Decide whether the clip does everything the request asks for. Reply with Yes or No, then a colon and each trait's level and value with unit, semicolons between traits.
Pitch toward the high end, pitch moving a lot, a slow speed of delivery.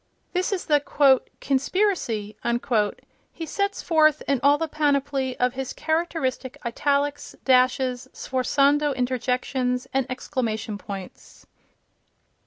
No: very high, 270 Hz; average, 2.8 semitones; slow, 100 wpm